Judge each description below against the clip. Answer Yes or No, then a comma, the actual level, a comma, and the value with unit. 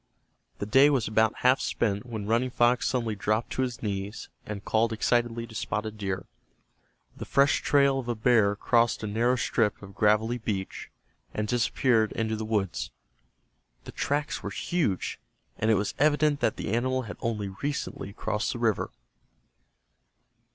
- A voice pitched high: No, low, 115 Hz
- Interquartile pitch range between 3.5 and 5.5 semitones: No, average, 2.8 semitones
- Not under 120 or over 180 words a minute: Yes, average, 160 wpm